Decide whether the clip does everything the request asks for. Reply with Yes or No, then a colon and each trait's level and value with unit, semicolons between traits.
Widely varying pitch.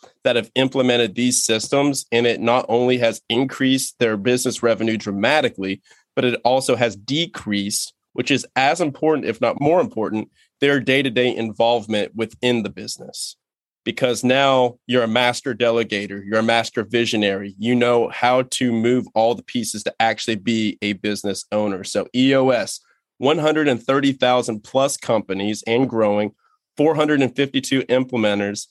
No: average, 3.0 semitones